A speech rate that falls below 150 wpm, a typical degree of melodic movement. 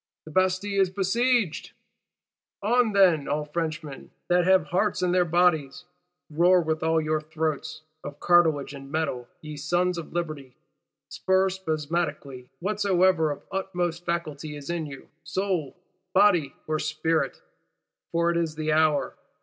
Yes: average, 140 wpm; average, 3.0 semitones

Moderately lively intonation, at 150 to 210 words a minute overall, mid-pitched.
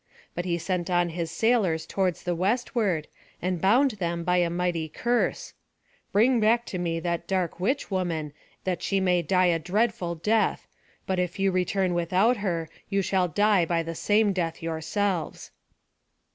Yes: average, 3.1 semitones; average, 165 wpm; medium, 180 Hz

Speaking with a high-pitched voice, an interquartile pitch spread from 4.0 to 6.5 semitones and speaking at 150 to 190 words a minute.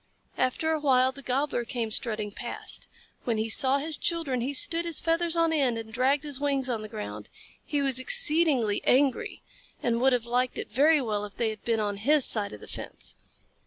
No: very high, 255 Hz; average, 4.5 semitones; fast, 205 wpm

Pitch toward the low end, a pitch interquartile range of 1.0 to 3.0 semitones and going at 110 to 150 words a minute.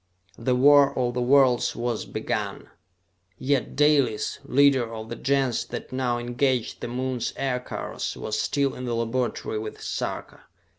Yes: low, 125 Hz; narrow, 2.4 semitones; average, 145 wpm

